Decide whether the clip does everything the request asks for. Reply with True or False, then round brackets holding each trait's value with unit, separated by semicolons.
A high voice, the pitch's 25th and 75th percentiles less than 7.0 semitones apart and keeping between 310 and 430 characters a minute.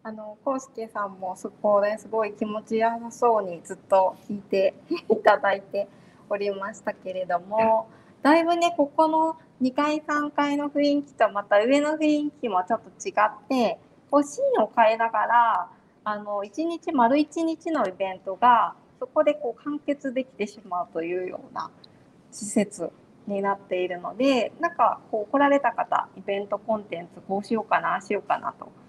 True (220 Hz; 6.1 semitones; 320 characters per minute)